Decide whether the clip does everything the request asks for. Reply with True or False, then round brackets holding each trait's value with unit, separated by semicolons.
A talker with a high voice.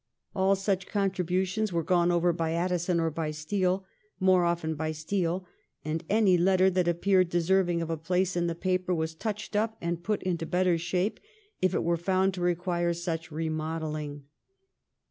False (175 Hz)